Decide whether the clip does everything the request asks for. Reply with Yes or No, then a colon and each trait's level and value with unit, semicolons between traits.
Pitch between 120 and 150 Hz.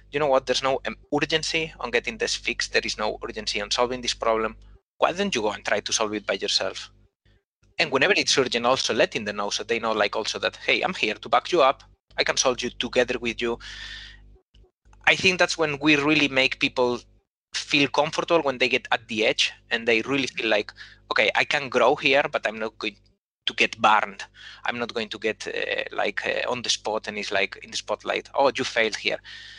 Yes: low, 135 Hz